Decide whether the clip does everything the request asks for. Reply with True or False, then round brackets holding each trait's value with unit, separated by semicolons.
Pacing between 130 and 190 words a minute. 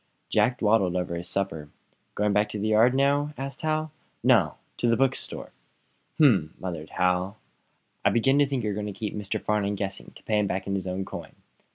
False (200 wpm)